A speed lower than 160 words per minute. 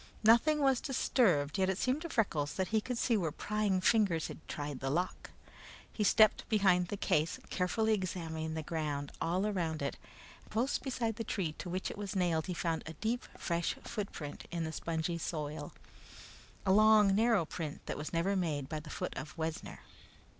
No: average, 190 wpm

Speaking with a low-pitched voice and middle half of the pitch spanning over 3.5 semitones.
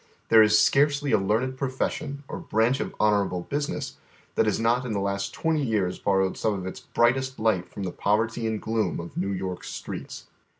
Yes: low, 110 Hz; average, 4.8 semitones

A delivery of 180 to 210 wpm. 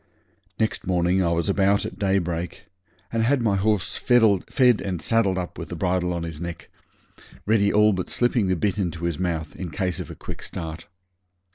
Yes: average, 185 wpm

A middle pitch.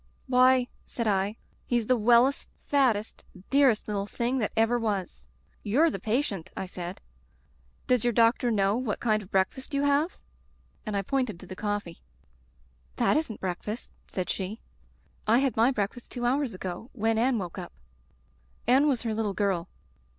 No: high, 225 Hz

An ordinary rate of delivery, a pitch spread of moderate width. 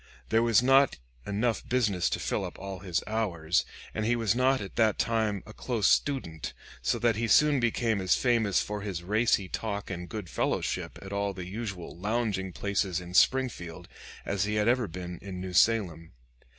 Yes: average, 185 wpm; average, 3.9 semitones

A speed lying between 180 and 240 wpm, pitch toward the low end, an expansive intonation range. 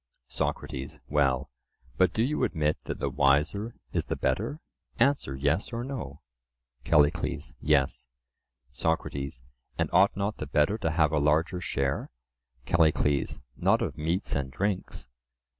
No: slow, 135 wpm; very low, 75 Hz; wide, 5.8 semitones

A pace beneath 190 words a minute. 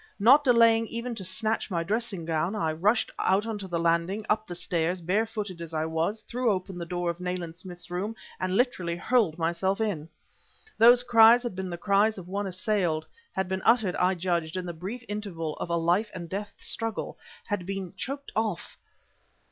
No: average, 195 wpm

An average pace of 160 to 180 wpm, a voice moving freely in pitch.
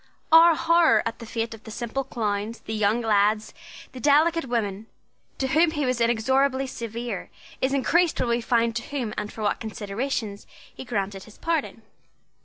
No: average, 175 wpm; average, 3.9 semitones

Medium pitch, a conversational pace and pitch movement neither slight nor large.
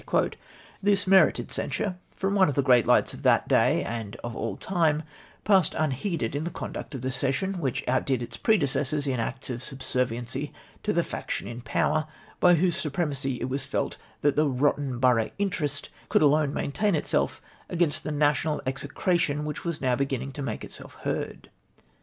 Yes: medium, 145 Hz; average, 180 wpm; average, 4.4 semitones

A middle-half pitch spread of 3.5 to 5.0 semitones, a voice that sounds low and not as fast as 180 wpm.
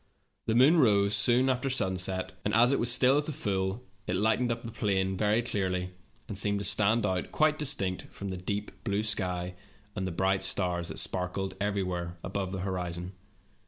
No: average, 3.8 semitones; low, 100 Hz; average, 185 wpm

